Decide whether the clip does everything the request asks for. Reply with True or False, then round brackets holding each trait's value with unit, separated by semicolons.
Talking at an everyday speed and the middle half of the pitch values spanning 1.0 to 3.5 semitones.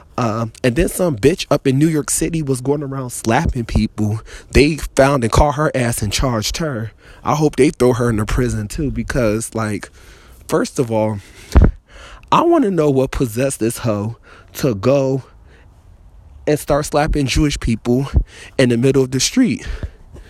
False (175 wpm; 5.1 semitones)